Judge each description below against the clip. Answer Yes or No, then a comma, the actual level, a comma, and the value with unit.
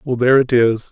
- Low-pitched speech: Yes, low, 125 Hz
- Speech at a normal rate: No, fast, 265 wpm